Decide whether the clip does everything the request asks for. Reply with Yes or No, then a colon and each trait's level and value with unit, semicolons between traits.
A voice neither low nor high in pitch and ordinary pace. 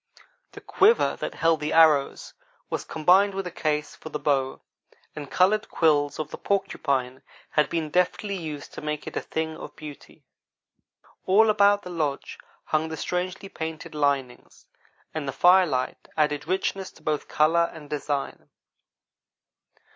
Yes: medium, 155 Hz; average, 150 wpm